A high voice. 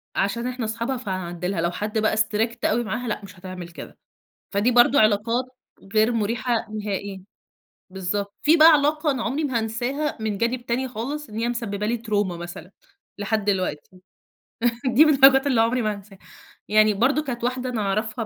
Yes: high, 220 Hz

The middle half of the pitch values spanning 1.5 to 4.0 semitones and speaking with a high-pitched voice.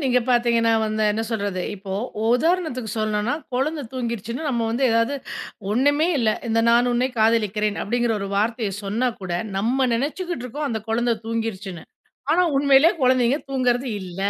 Yes: average, 3.1 semitones; high, 235 Hz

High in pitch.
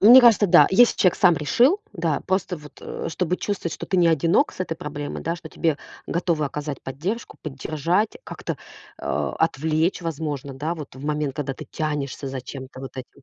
No: medium, 160 Hz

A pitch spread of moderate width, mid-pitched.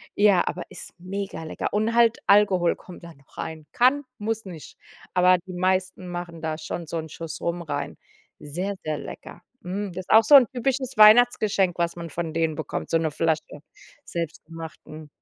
Yes: average, 4.2 semitones; medium, 175 Hz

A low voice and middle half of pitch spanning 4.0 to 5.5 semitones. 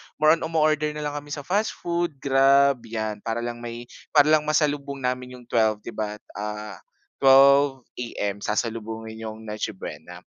Yes: low, 125 Hz; average, 4.8 semitones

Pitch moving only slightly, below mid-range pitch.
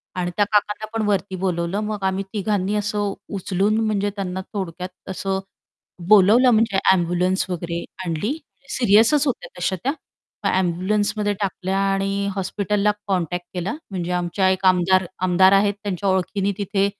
No: narrow, 2.2 semitones; high, 195 Hz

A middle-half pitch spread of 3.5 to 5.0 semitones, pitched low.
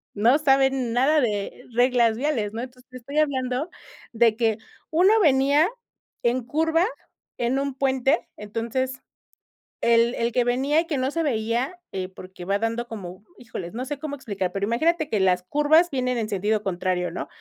No: average, 4.2 semitones; very high, 250 Hz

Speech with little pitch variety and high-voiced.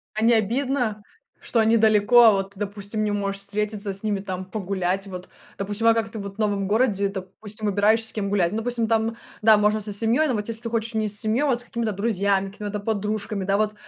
Yes: narrow, 2.0 semitones; high, 210 Hz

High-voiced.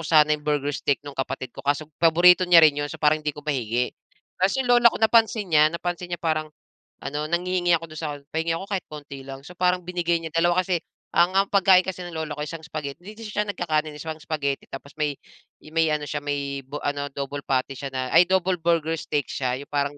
No: medium, 155 Hz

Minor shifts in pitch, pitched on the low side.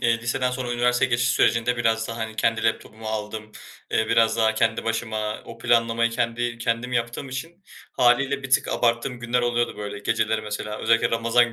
Yes: narrow, 1.4 semitones; low, 115 Hz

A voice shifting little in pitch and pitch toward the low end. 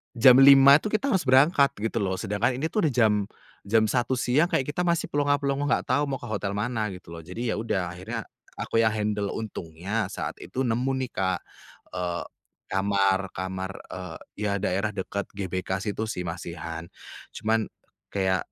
No: wide, 5.6 semitones; low, 110 Hz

